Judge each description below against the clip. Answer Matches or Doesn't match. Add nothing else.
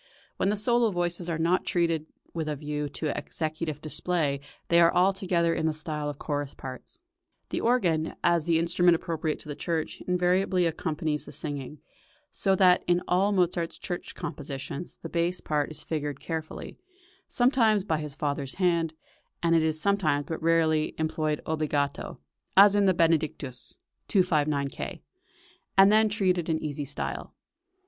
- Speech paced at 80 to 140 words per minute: Doesn't match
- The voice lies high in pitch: Doesn't match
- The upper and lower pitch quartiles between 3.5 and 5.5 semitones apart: Doesn't match